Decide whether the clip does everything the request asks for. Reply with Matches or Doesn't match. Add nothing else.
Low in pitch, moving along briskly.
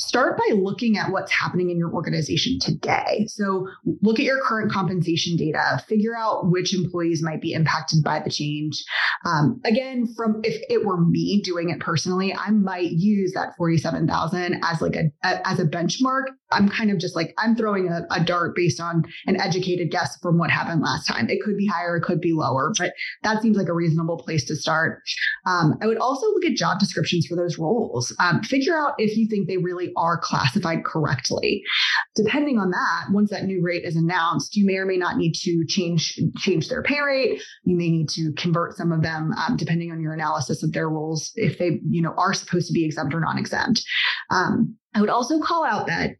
Doesn't match